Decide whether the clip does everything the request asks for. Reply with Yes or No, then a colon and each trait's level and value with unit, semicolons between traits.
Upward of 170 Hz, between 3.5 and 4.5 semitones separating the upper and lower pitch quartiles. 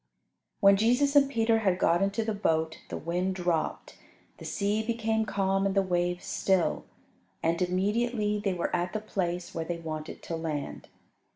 Yes: high, 190 Hz; average, 3.9 semitones